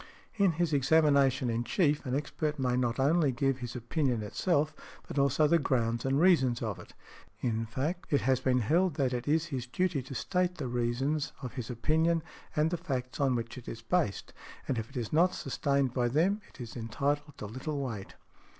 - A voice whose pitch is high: No, low, 135 Hz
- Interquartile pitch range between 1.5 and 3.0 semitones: No, average, 4.1 semitones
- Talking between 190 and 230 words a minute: Yes, average, 200 wpm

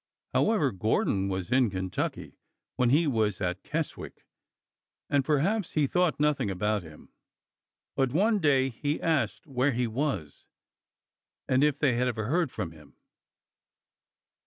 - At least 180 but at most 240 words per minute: No, slow, 135 wpm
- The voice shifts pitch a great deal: Yes, wide, 6.2 semitones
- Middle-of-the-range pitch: No, low, 130 Hz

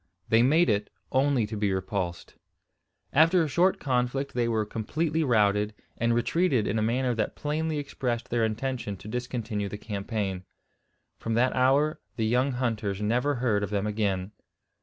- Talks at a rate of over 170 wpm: No, average, 160 wpm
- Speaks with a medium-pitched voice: No, low, 115 Hz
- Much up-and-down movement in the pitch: No, average, 4.1 semitones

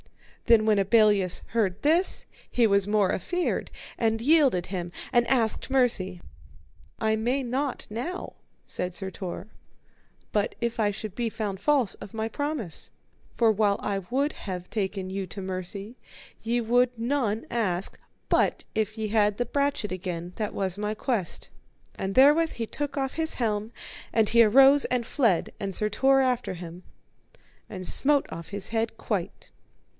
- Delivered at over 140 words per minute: Yes, average, 160 wpm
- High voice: Yes, high, 220 Hz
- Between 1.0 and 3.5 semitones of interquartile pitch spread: No, average, 4.1 semitones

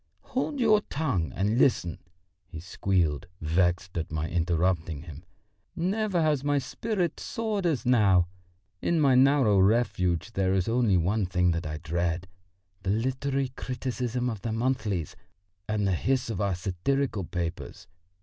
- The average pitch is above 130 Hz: No, low, 105 Hz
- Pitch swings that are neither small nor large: No, wide, 7.2 semitones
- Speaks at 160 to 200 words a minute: No, average, 145 wpm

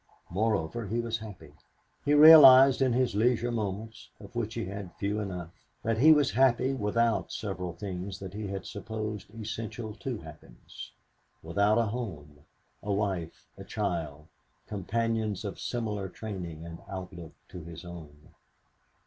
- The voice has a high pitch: No, low, 105 Hz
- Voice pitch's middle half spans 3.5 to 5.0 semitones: Yes, average, 3.9 semitones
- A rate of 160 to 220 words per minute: No, average, 145 wpm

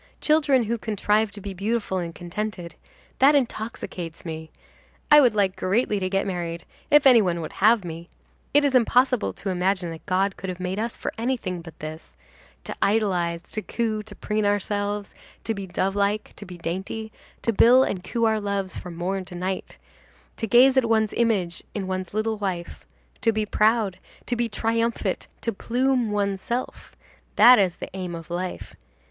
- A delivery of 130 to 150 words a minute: No, average, 175 wpm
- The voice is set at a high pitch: Yes, high, 205 Hz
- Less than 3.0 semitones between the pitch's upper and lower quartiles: No, average, 3.8 semitones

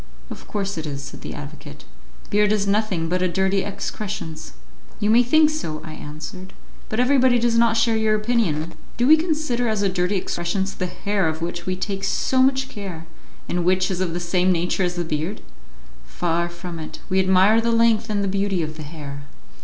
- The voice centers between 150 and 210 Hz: Yes, high, 190 Hz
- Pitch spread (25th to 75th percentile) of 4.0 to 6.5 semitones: Yes, average, 4.3 semitones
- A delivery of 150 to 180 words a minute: No, average, 200 wpm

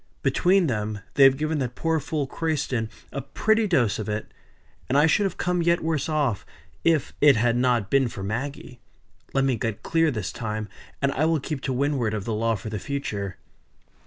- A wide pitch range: Yes, wide, 5.8 semitones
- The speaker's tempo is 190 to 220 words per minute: Yes, average, 200 wpm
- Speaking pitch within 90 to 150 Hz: Yes, low, 135 Hz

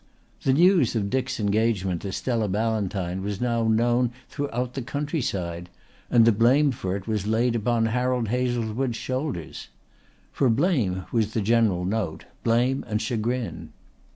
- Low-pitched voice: Yes, low, 115 Hz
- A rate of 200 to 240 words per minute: No, average, 145 wpm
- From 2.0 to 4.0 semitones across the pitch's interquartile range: Yes, average, 3.4 semitones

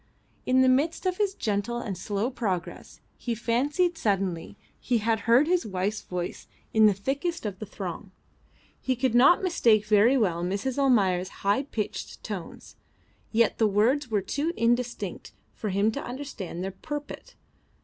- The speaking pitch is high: Yes, high, 225 Hz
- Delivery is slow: No, average, 160 wpm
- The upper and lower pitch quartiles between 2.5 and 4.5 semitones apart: No, average, 5.0 semitones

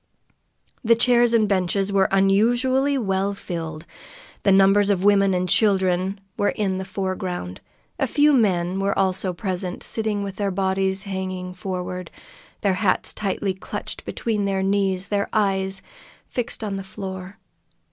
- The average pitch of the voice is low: No, high, 195 Hz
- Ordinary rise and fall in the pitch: No, narrow, 1.5 semitones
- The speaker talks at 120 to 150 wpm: Yes, average, 140 wpm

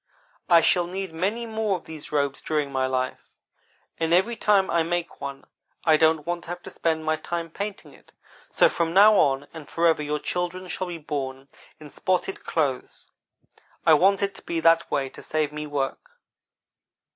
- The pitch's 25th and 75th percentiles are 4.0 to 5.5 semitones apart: No, average, 3.5 semitones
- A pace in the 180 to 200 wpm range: Yes, average, 185 wpm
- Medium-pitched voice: Yes, medium, 165 Hz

